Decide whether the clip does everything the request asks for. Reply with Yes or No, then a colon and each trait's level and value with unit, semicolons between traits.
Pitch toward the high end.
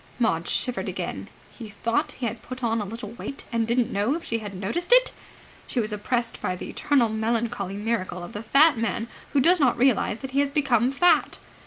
Yes: high, 235 Hz